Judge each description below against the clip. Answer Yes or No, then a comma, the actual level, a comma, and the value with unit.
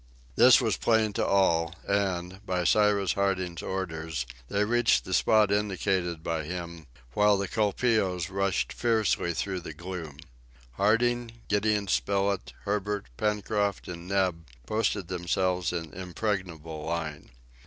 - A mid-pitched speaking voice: No, very low, 95 Hz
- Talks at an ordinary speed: No, slow, 125 wpm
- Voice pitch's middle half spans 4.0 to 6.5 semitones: No, average, 3.3 semitones